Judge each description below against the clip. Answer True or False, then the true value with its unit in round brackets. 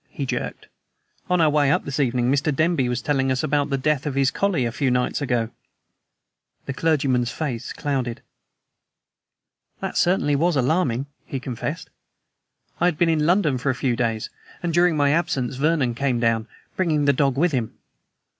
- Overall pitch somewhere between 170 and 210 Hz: False (140 Hz)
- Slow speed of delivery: False (175 wpm)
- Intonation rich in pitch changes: False (3.6 semitones)